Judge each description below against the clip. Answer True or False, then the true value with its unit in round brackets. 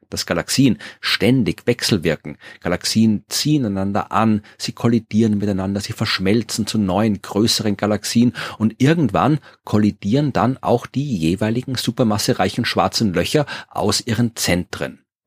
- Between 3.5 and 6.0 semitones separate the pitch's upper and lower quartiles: False (2.8 semitones)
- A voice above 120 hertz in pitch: False (110 Hz)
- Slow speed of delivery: True (120 wpm)